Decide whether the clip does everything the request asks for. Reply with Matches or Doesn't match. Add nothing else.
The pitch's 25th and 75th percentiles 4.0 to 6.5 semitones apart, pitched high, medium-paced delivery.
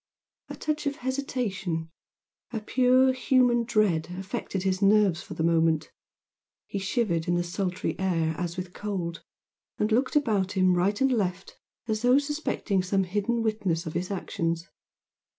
Matches